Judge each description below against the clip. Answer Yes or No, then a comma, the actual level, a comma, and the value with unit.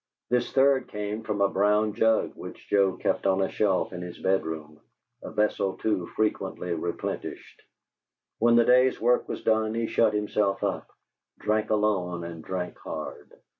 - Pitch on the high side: No, low, 105 Hz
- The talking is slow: No, average, 160 wpm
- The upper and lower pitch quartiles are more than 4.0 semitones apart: No, average, 2.8 semitones